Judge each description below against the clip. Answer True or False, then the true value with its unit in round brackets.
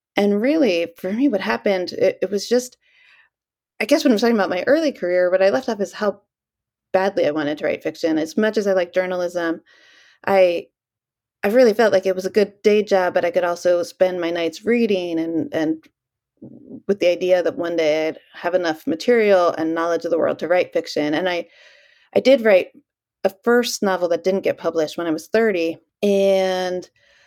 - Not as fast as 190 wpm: False (205 wpm)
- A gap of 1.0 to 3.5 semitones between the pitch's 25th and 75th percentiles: False (4.3 semitones)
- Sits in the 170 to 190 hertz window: True (185 Hz)